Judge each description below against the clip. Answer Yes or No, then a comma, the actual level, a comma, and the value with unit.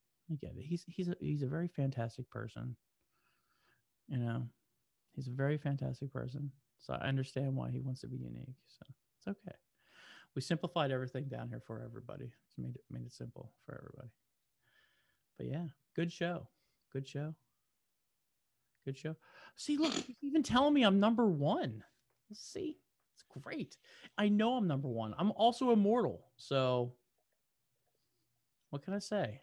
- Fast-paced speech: No, average, 160 wpm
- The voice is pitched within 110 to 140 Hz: Yes, low, 135 Hz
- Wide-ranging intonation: Yes, wide, 6.5 semitones